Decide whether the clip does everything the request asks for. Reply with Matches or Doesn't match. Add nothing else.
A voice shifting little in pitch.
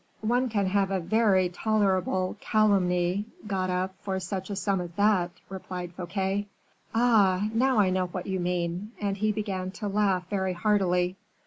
Matches